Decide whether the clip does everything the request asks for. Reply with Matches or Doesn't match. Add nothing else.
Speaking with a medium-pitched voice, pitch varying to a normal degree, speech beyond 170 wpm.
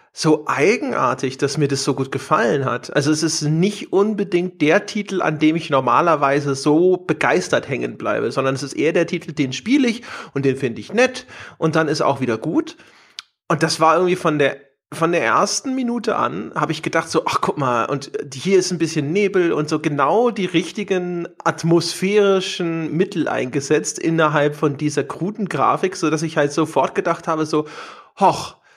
Matches